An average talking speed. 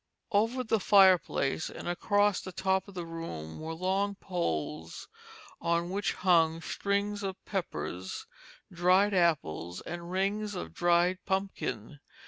No: slow, 125 wpm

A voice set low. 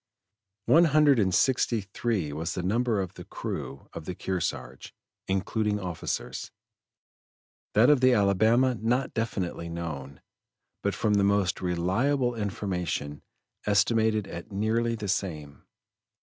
Yes: low, 100 Hz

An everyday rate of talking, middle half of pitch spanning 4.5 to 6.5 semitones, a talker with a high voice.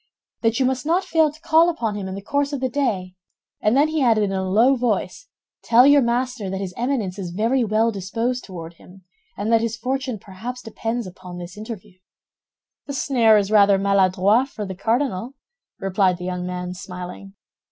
Yes: average, 195 wpm; average, 5.0 semitones; high, 220 Hz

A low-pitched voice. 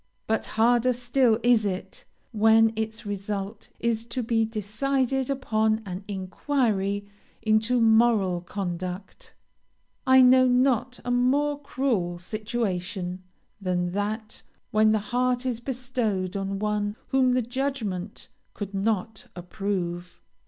No: high, 220 Hz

